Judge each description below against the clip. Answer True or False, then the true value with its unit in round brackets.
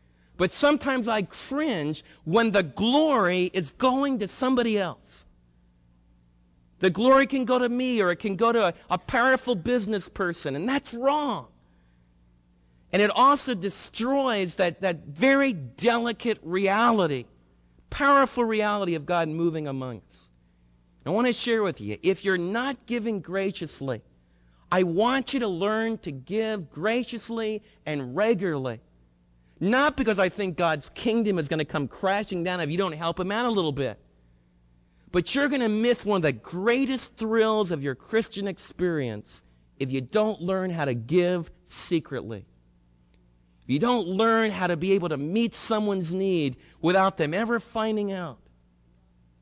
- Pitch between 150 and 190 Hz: True (185 Hz)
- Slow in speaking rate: False (155 wpm)